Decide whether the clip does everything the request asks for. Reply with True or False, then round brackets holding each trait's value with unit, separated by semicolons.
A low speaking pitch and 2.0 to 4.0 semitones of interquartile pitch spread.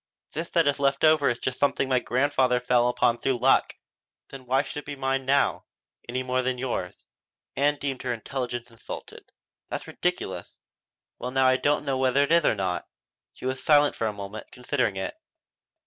True (130 Hz; 2.4 semitones)